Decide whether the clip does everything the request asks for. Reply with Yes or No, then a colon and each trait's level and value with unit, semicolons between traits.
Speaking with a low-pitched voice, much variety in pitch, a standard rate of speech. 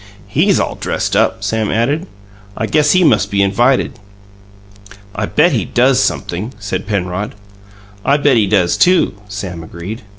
Yes: low, 110 Hz; wide, 6.0 semitones; average, 155 wpm